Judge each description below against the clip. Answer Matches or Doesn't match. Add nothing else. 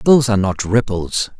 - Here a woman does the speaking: Doesn't match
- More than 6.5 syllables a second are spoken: Doesn't match